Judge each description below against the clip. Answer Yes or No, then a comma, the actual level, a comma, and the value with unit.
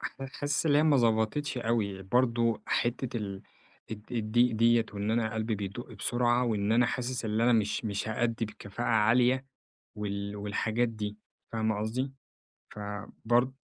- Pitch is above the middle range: No, low, 115 Hz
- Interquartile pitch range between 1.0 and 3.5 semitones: Yes, narrow, 2.5 semitones